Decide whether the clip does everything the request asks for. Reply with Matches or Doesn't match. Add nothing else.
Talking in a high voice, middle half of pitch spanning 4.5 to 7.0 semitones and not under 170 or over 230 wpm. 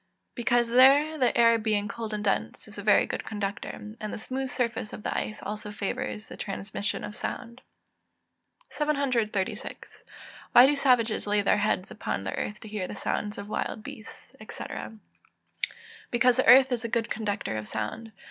Doesn't match